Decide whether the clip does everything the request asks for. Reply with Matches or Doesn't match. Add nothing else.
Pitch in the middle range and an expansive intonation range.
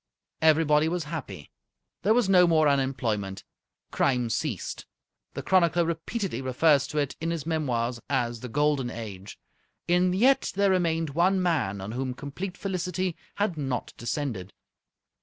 Matches